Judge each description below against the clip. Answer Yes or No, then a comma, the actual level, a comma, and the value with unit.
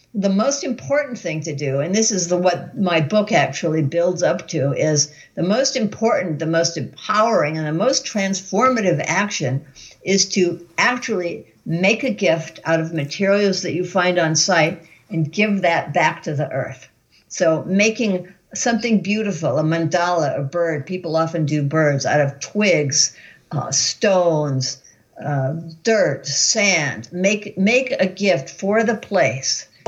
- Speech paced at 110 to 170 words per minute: Yes, average, 155 wpm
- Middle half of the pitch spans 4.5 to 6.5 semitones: Yes, average, 4.8 semitones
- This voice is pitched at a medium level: Yes, medium, 175 Hz